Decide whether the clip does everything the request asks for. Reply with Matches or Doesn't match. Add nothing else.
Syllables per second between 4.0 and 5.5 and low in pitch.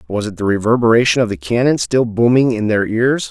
Doesn't match